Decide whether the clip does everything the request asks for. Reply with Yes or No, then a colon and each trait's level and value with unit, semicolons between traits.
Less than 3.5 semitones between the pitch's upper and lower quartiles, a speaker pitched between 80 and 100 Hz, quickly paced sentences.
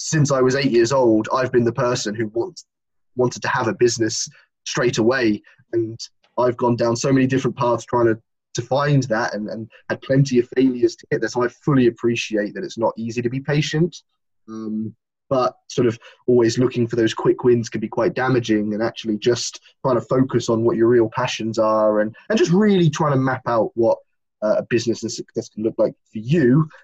No: average, 2.8 semitones; low, 120 Hz; fast, 215 wpm